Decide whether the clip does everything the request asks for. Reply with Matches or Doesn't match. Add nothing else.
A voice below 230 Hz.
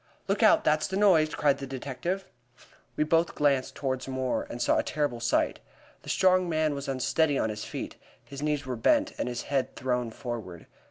Matches